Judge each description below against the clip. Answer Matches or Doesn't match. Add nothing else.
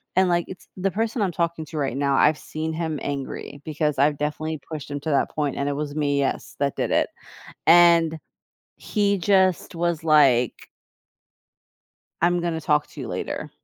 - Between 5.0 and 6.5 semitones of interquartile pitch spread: Doesn't match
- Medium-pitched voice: Matches